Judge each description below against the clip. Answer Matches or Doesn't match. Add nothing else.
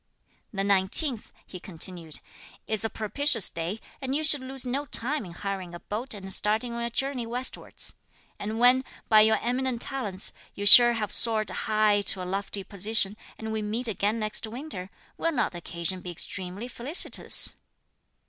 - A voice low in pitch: Doesn't match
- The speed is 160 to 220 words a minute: Matches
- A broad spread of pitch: Doesn't match